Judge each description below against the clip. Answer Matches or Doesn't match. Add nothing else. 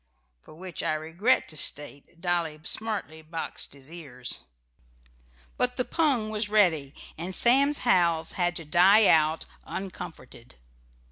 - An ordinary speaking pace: Doesn't match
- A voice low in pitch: Doesn't match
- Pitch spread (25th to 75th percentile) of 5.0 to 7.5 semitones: Matches